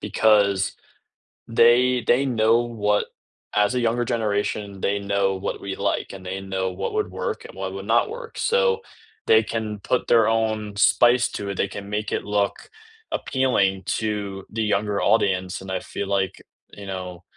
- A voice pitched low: Yes, low, 105 Hz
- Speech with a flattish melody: No, average, 3.3 semitones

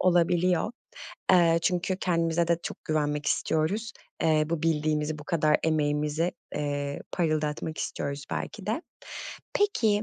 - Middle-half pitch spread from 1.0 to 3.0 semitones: Yes, narrow, 2.6 semitones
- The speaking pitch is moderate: Yes, medium, 160 Hz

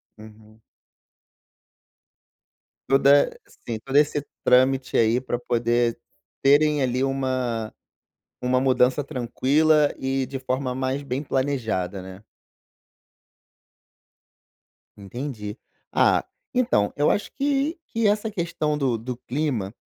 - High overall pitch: No, low, 130 Hz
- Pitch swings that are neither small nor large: Yes, average, 3.4 semitones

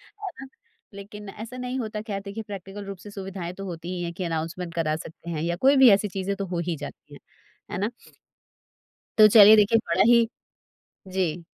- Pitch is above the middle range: Yes, high, 195 Hz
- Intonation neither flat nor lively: Yes, average, 3.7 semitones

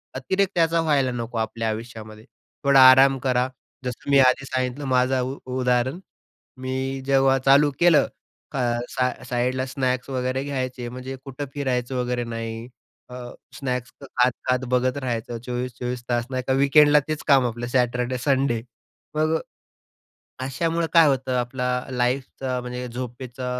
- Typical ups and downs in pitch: No, narrow, 1.7 semitones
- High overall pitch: No, low, 130 Hz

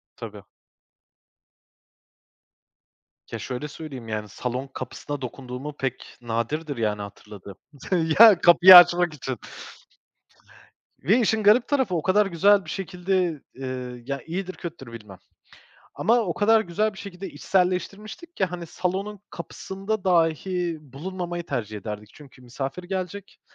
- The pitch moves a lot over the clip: Yes, wide, 6.8 semitones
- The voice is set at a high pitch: No, medium, 170 Hz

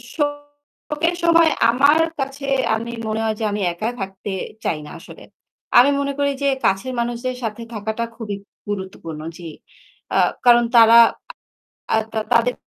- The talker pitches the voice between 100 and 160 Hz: No, high, 235 Hz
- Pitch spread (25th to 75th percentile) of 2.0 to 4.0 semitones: No, average, 4.9 semitones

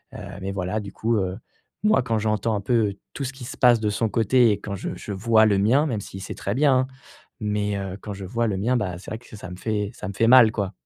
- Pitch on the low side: Yes, low, 105 Hz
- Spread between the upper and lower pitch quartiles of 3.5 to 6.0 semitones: No, average, 2.9 semitones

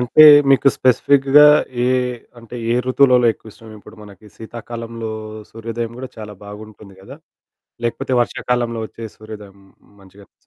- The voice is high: No, low, 115 Hz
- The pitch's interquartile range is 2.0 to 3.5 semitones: Yes, narrow, 2.5 semitones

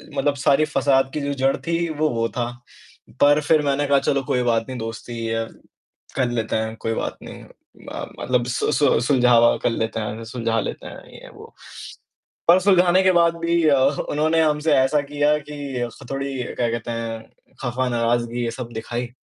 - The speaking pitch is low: Yes, low, 130 Hz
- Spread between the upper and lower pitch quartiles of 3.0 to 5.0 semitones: Yes, average, 4.1 semitones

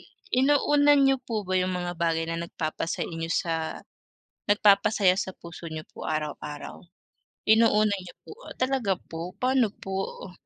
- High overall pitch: Yes, high, 195 Hz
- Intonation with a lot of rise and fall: Yes, wide, 6.8 semitones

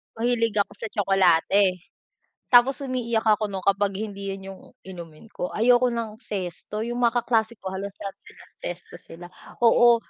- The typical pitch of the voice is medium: No, high, 210 Hz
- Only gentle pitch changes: No, average, 3.4 semitones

